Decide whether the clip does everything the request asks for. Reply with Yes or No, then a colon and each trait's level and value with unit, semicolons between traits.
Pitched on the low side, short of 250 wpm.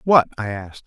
Yes: low, 120 Hz; fast, 205 wpm